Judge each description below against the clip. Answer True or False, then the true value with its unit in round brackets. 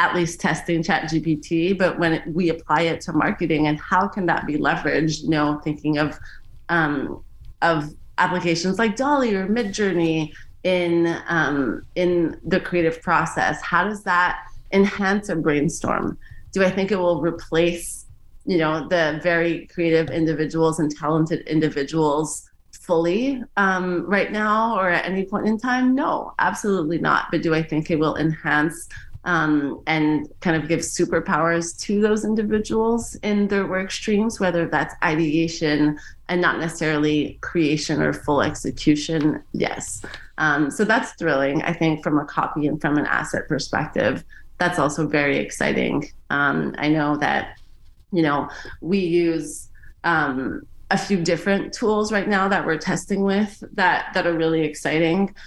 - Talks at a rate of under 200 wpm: True (155 wpm)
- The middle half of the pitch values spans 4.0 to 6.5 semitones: False (3.6 semitones)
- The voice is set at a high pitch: False (165 Hz)